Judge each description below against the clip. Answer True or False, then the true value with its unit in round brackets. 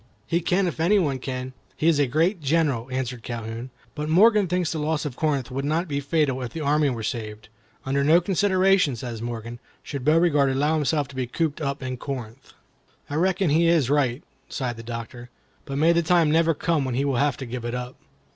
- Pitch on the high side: False (140 Hz)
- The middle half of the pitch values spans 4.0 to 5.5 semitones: True (4.5 semitones)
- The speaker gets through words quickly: True (220 wpm)